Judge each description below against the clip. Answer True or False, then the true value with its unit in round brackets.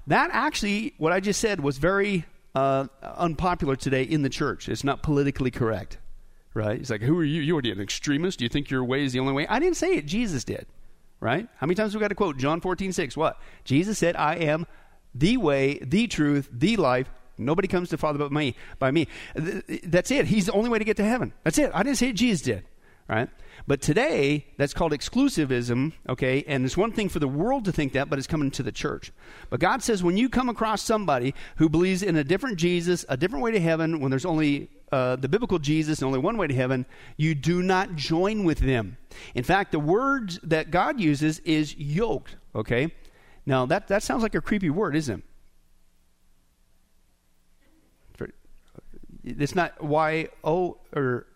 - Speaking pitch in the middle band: True (155 Hz)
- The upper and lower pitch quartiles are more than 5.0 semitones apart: True (5.6 semitones)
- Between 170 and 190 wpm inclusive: False (205 wpm)